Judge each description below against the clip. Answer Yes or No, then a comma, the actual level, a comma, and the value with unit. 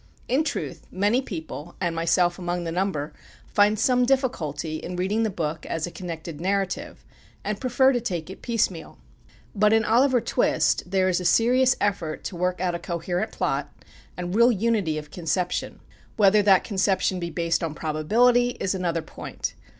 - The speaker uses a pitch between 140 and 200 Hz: Yes, medium, 185 Hz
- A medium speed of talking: Yes, average, 170 wpm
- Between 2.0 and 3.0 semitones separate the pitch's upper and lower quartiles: No, average, 4.6 semitones